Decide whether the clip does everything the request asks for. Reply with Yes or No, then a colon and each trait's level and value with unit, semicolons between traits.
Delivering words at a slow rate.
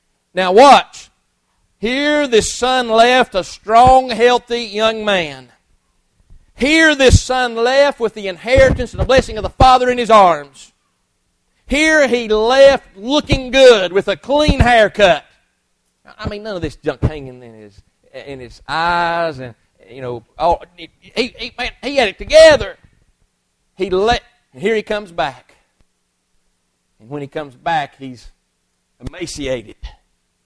No: average, 145 wpm